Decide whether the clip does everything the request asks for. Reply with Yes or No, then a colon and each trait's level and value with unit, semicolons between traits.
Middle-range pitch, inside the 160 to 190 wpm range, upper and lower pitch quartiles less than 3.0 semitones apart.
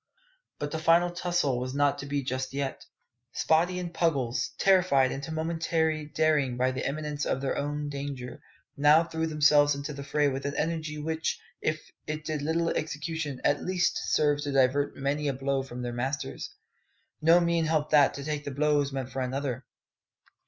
Yes: medium, 145 Hz; average, 180 wpm; narrow, 2.6 semitones